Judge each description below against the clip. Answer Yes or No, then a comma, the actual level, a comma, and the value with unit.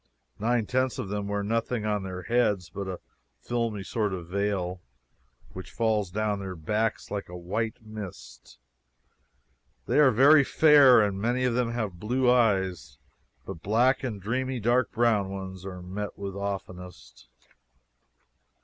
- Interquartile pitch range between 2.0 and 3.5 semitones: No, average, 3.9 semitones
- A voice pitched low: Yes, low, 105 Hz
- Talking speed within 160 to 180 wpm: No, average, 150 wpm